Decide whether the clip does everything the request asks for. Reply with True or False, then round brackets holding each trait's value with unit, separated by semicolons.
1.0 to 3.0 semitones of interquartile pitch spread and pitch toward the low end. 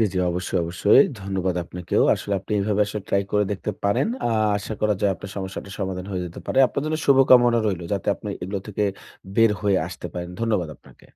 True (2.4 semitones; 100 Hz)